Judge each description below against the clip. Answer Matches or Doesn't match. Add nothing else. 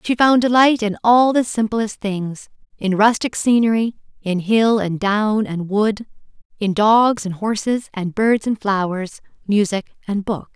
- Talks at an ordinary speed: Matches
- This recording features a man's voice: Doesn't match